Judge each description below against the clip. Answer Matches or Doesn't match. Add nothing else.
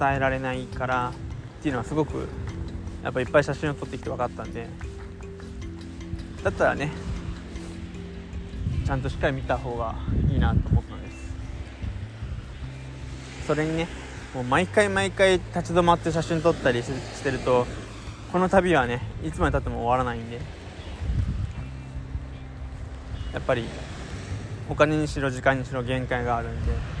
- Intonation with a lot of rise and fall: Matches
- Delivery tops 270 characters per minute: Matches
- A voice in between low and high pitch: Doesn't match